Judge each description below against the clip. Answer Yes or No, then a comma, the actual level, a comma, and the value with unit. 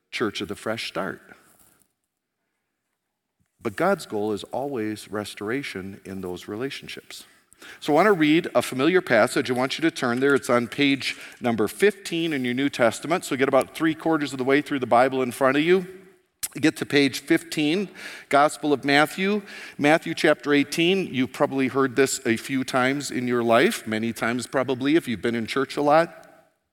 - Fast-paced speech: No, average, 190 wpm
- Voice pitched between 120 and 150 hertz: Yes, medium, 140 Hz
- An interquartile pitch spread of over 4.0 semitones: Yes, average, 4.5 semitones